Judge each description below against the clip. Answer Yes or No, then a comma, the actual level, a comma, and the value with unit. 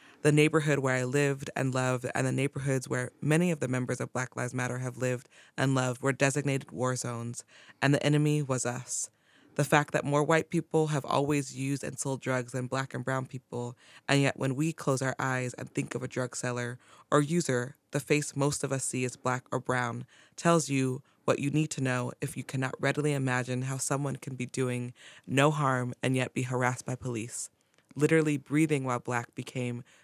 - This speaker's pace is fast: Yes, fast, 210 wpm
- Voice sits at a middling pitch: No, low, 130 Hz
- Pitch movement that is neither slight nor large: No, narrow, 2.3 semitones